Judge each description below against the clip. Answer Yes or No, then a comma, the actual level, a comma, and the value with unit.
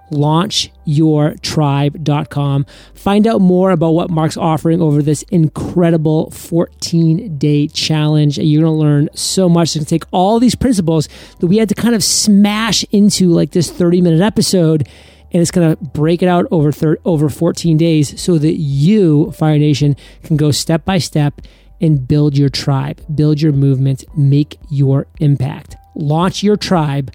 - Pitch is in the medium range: Yes, medium, 160 Hz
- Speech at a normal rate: Yes, average, 170 wpm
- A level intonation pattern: No, average, 3.0 semitones